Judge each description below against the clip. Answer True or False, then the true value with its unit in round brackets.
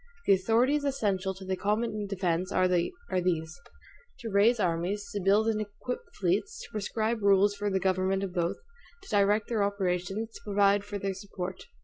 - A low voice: False (200 Hz)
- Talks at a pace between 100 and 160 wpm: False (170 wpm)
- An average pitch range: False (2.3 semitones)